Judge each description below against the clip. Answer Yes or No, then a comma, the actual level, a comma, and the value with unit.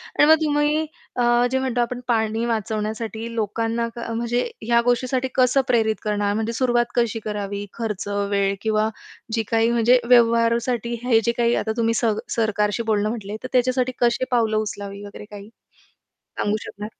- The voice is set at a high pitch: Yes, high, 230 Hz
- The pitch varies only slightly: Yes, narrow, 2.0 semitones